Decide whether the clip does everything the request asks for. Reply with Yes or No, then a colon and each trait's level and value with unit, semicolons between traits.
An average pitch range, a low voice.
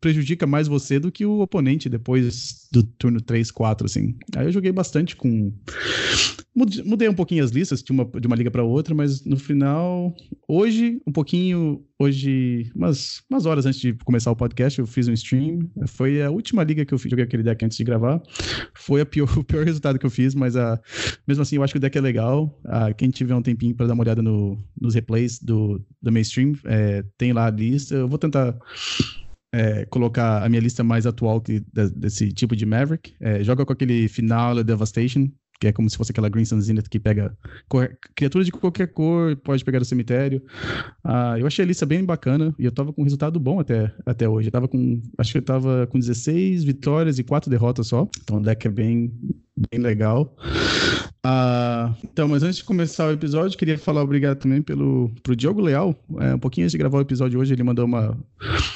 Yes: average, 4.1 semitones; low, 130 Hz